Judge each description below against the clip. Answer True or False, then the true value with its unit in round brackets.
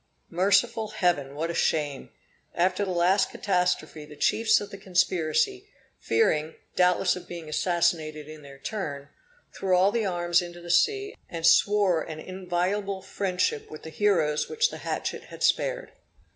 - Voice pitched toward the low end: False (180 Hz)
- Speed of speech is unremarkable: True (150 wpm)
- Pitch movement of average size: True (4.0 semitones)